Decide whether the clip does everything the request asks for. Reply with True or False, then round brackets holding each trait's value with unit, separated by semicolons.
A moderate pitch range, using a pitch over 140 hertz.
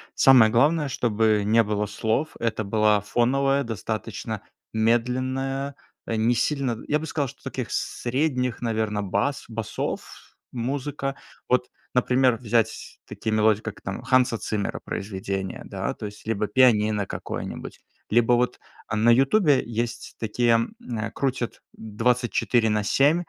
False (3.2 semitones; 120 Hz)